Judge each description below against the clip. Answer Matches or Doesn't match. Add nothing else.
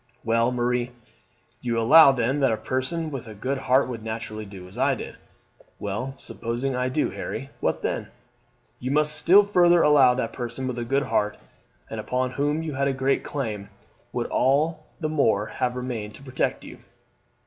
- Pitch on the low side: Matches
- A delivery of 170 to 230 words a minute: Matches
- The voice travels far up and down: Doesn't match